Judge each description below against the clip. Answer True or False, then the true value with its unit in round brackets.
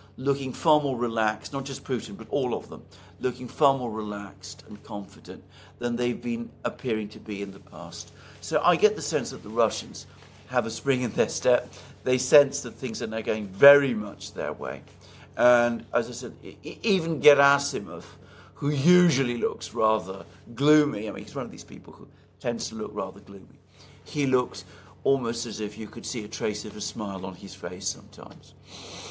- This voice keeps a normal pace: True (190 wpm)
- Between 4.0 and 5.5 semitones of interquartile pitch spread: True (5.1 semitones)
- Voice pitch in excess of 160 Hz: False (115 Hz)